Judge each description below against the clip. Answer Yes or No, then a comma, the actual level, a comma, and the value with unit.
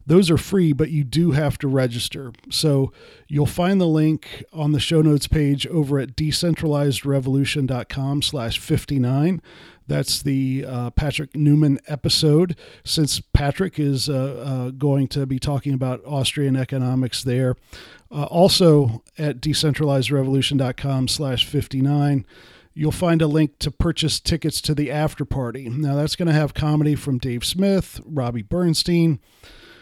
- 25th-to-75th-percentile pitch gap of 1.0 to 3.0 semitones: Yes, narrow, 2.6 semitones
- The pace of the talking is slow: No, average, 145 wpm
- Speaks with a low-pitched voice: No, medium, 145 Hz